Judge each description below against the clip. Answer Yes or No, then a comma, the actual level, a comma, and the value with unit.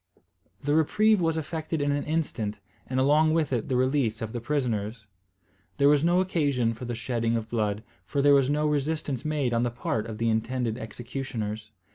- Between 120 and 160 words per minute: No, average, 190 wpm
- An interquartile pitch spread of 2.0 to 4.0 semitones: No, average, 4.6 semitones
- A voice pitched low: Yes, low, 130 Hz